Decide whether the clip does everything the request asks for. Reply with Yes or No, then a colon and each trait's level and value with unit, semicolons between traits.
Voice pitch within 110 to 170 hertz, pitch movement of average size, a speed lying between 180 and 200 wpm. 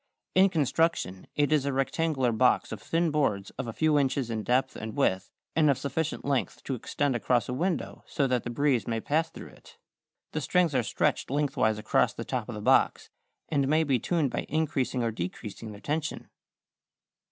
Yes: low, 135 Hz; average, 4.5 semitones; average, 195 wpm